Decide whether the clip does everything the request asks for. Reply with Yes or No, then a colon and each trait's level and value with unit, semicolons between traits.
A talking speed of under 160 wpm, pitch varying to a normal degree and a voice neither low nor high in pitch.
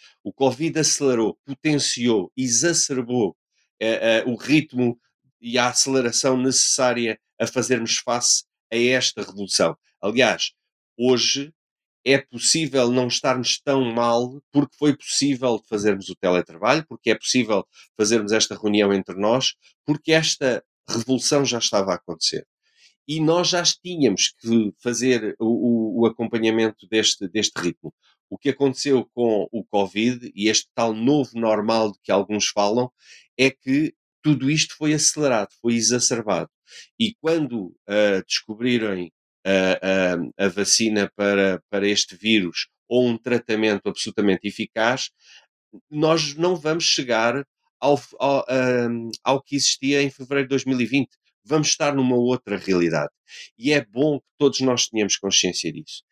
No: average, 140 wpm; average, 4.1 semitones; low, 120 Hz